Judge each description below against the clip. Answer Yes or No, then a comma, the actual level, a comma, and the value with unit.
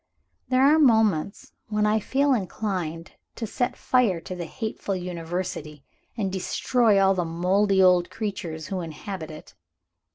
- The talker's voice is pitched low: No, high, 190 Hz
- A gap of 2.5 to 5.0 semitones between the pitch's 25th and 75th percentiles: Yes, average, 4.1 semitones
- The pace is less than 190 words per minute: Yes, average, 140 wpm